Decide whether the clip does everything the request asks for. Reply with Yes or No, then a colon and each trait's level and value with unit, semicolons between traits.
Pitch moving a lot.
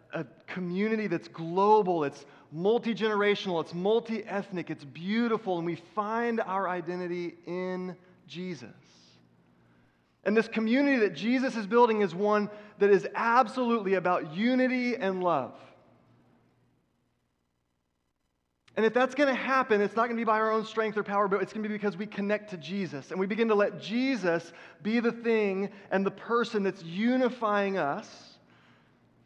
No: average, 4.7 semitones